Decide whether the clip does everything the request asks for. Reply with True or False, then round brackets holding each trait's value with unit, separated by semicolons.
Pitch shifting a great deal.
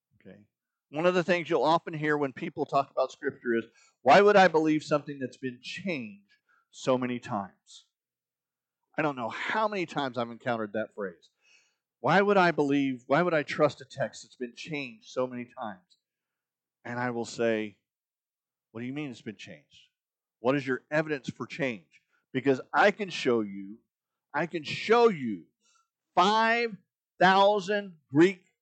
True (6.9 semitones)